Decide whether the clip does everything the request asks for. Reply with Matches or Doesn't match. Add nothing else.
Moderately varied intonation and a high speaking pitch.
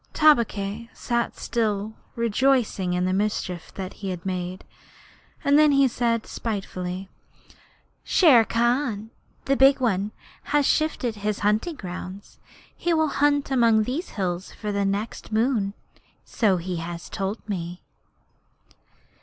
Matches